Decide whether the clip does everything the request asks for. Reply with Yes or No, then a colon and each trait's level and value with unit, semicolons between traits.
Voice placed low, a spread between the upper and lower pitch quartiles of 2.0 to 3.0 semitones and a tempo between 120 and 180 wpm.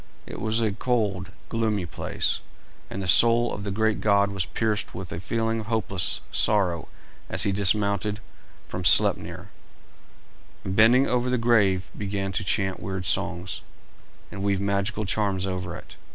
Yes: low, 100 Hz; narrow, 2.6 semitones; average, 155 wpm